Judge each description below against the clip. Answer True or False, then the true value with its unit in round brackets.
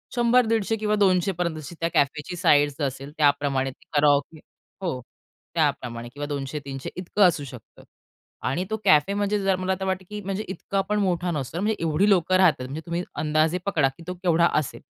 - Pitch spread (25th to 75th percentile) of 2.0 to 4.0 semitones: False (5.0 semitones)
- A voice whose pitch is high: False (170 Hz)